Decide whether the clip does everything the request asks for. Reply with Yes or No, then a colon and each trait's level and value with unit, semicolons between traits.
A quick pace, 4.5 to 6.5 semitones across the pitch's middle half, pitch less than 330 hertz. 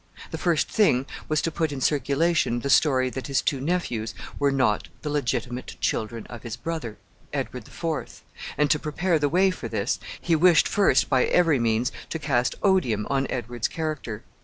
No: average, 185 wpm; average, 4.9 semitones; medium, 140 Hz